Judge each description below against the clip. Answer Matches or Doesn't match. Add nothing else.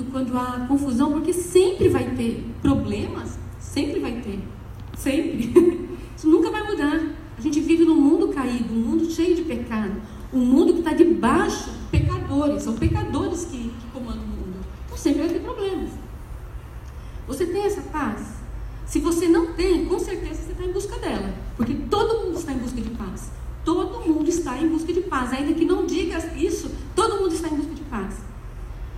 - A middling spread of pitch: Matches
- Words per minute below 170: Doesn't match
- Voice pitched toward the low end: Doesn't match